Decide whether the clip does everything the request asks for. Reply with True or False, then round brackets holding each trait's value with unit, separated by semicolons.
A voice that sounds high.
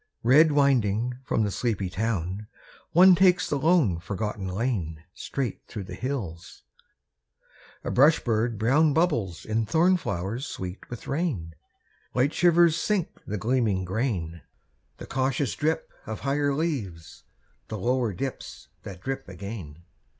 False (120 Hz)